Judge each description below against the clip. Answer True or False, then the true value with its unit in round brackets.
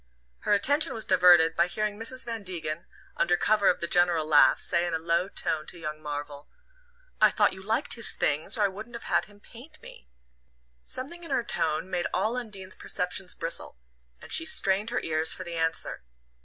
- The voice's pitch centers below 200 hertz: True (185 Hz)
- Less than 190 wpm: False (195 wpm)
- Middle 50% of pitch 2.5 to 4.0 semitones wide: False (5.2 semitones)